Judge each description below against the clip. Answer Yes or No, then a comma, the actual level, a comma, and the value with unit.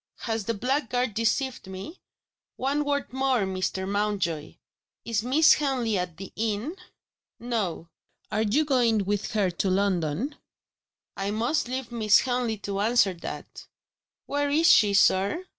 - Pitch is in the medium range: No, high, 220 Hz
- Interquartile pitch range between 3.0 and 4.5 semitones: No, average, 4.9 semitones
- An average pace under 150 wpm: Yes, average, 140 wpm